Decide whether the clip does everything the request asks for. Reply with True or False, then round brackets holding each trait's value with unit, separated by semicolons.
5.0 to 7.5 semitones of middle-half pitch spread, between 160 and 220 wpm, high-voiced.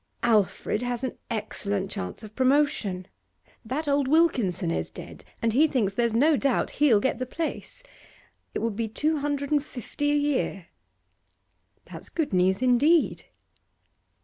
False (5.6 semitones; 150 wpm; 250 Hz)